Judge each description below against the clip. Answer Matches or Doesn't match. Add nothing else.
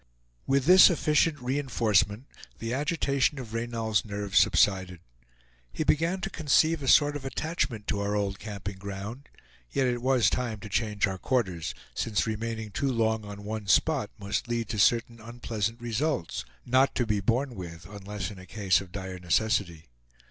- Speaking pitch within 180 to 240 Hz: Doesn't match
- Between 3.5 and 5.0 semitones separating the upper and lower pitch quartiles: Matches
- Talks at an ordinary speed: Matches